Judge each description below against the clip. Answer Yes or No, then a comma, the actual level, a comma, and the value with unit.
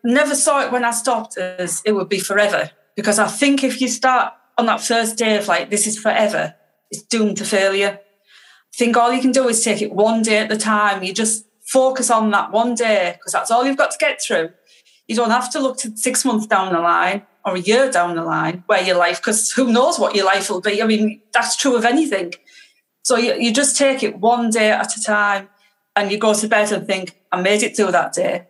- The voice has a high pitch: Yes, high, 220 Hz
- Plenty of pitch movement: No, average, 3.2 semitones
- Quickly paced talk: Yes, fast, 245 wpm